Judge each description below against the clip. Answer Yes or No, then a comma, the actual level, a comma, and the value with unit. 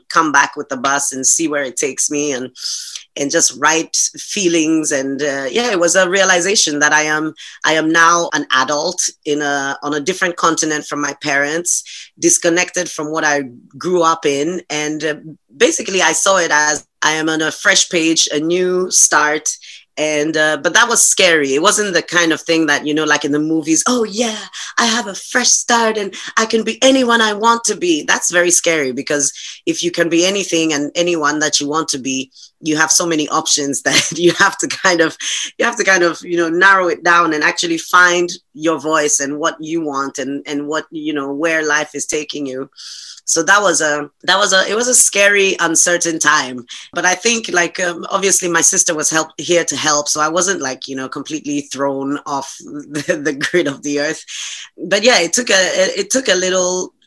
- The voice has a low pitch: No, medium, 160 Hz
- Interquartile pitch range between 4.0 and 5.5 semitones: No, average, 3.5 semitones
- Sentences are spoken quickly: Yes, fast, 215 wpm